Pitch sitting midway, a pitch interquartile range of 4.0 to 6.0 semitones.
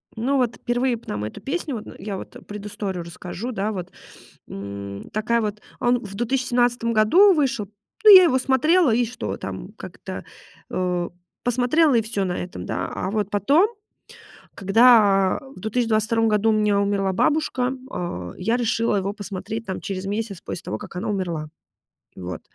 No: high, 215 Hz; average, 4.3 semitones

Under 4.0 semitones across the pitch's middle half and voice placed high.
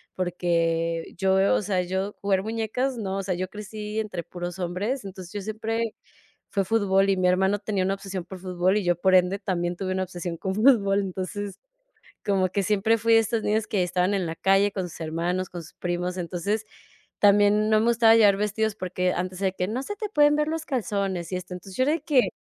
Yes: average, 2.8 semitones; high, 195 Hz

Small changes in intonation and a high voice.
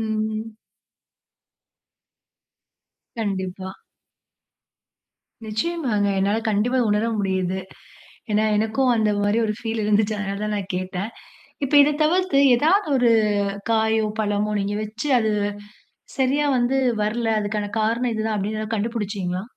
Yes: narrow, 2.2 semitones; high, 215 Hz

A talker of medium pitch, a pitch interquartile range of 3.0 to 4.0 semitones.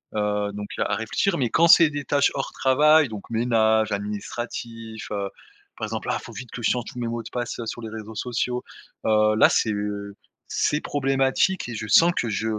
No: low, 115 Hz; average, 3.5 semitones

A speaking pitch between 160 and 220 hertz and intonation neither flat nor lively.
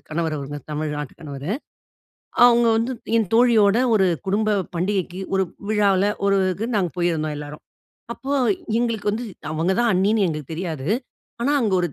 No: high, 190 Hz; wide, 5.7 semitones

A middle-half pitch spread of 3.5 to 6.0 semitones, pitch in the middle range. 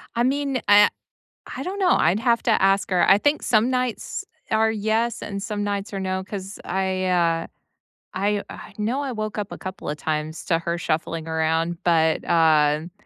No: average, 4.7 semitones; high, 195 Hz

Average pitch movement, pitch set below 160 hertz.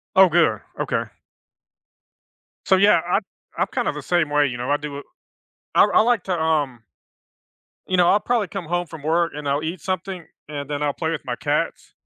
No: average, 4.0 semitones; medium, 165 Hz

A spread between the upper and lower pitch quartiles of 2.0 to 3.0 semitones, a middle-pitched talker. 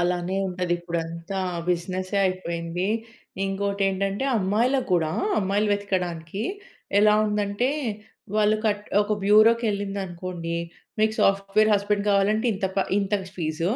No: average, 2.7 semitones; high, 195 Hz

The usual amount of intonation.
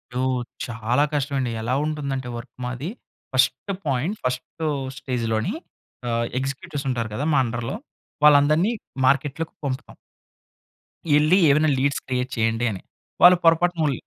Yes: average, 3.5 semitones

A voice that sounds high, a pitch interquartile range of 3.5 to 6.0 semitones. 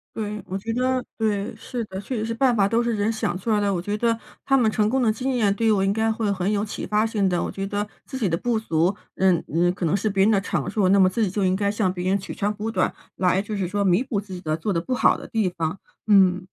No: high, 205 Hz; average, 2.9 semitones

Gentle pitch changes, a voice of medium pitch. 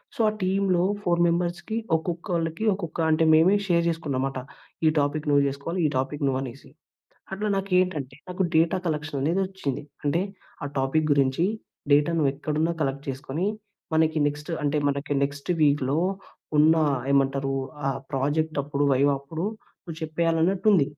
No: average, 3.3 semitones; medium, 155 Hz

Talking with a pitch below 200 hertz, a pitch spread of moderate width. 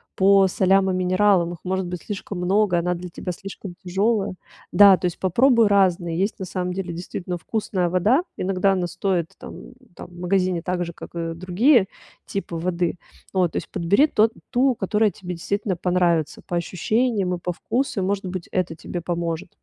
No: medium, 185 Hz; narrow, 2.2 semitones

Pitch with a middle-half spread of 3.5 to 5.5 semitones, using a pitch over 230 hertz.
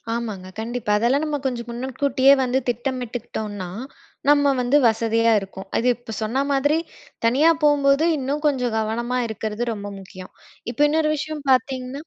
Yes: average, 3.9 semitones; very high, 250 Hz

